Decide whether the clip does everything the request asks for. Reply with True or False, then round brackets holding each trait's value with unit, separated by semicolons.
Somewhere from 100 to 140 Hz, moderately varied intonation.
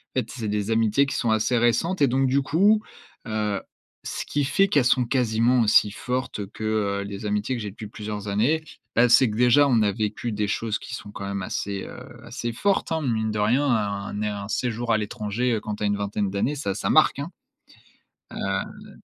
True (115 Hz; 3.7 semitones)